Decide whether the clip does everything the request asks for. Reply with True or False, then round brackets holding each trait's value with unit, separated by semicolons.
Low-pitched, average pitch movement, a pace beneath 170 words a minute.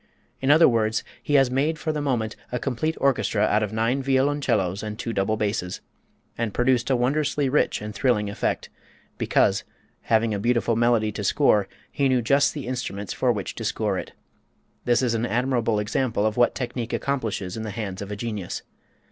False (115 Hz; 3.8 semitones; 190 wpm)